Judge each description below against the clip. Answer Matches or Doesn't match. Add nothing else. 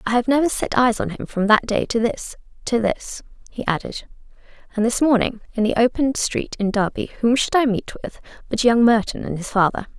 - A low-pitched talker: Doesn't match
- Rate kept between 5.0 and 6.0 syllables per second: Matches